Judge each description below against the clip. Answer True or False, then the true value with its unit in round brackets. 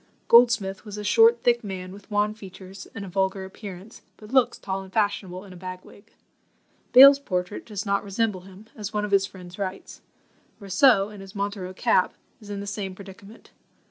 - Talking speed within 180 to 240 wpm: True (190 wpm)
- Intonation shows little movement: True (1.9 semitones)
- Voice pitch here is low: False (200 Hz)